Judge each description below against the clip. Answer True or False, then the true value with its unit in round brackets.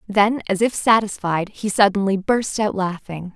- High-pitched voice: True (200 Hz)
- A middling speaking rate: True (160 wpm)